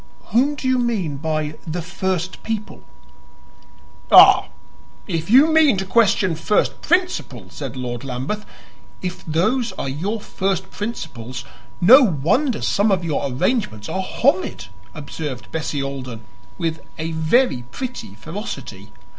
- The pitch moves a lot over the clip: Yes, wide, 7.9 semitones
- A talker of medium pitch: Yes, medium, 175 Hz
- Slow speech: Yes, slow, 130 wpm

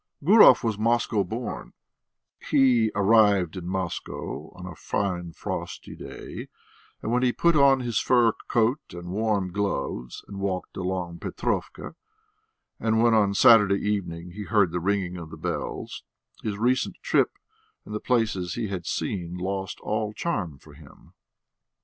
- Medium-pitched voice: No, low, 100 Hz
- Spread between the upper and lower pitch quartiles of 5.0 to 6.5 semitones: No, average, 4.0 semitones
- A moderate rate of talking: Yes, average, 150 wpm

